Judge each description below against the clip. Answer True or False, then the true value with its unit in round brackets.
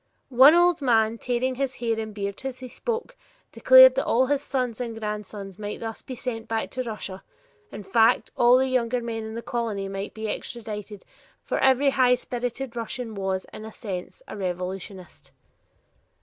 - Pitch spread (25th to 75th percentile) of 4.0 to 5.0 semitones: False (3.4 semitones)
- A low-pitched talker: False (230 Hz)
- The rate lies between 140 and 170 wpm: False (185 wpm)